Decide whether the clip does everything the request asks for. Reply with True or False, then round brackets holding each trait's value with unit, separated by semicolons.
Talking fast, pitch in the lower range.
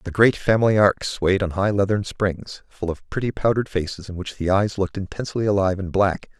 True (215 wpm; 100 Hz)